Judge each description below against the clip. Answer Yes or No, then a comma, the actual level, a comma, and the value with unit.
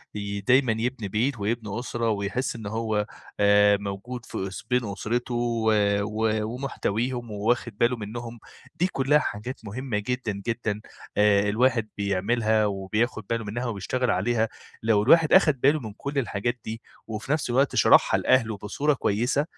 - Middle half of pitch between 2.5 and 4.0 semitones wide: Yes, average, 3.2 semitones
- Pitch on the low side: Yes, low, 115 Hz